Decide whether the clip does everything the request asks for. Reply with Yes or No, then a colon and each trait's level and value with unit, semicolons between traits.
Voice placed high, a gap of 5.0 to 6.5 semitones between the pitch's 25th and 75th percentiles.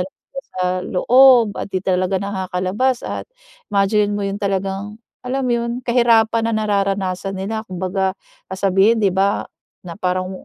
No: high, 200 Hz; average, 2.9 semitones